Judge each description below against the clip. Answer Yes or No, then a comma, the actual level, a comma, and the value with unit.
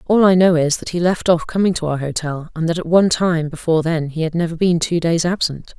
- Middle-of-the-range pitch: Yes, medium, 165 Hz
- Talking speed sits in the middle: No, fast, 270 wpm